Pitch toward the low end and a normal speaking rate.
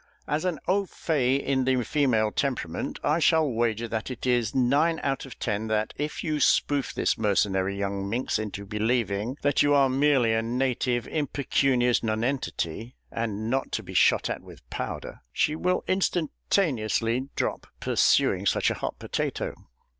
Yes: low, 125 Hz; average, 160 wpm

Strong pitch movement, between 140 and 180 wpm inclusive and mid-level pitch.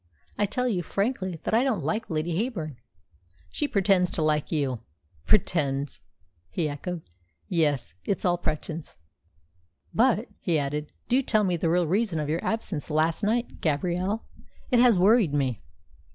Yes: wide, 5.7 semitones; average, 150 wpm; medium, 175 Hz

